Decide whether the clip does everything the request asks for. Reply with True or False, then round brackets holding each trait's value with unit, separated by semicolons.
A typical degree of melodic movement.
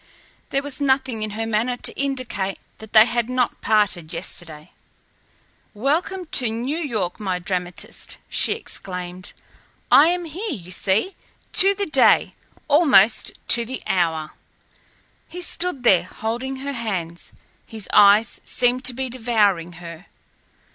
False (6.1 semitones)